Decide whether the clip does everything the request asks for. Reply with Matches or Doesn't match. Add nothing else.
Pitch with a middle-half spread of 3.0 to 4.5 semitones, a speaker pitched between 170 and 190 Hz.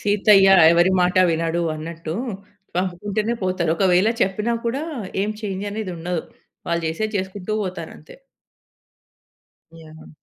Matches